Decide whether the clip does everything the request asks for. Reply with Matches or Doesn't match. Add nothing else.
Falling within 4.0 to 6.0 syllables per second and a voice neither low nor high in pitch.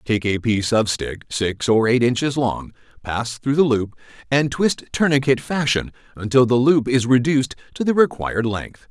Doesn't match